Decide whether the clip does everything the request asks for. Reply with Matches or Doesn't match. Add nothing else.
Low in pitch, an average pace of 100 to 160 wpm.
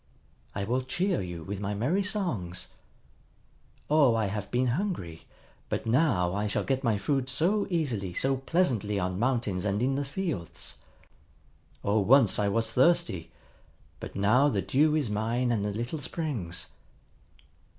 Matches